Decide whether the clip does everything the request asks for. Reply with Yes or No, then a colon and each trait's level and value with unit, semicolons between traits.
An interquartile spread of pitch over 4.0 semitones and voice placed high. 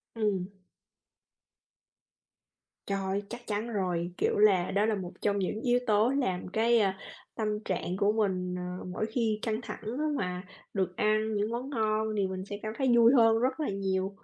No: average, 2.9 semitones; high, 210 Hz